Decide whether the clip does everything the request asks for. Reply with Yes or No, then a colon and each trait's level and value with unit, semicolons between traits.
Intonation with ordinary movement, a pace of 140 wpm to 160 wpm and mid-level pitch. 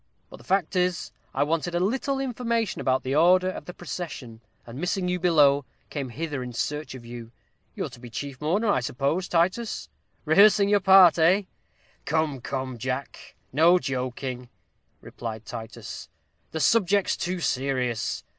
No: wide, 6.1 semitones; average, 155 wpm; medium, 160 Hz